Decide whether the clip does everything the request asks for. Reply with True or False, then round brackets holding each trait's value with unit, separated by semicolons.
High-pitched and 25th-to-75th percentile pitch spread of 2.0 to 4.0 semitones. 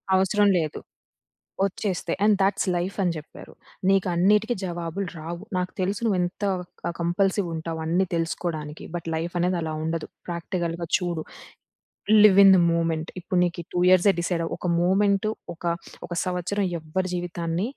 False (175 Hz; 2.4 semitones)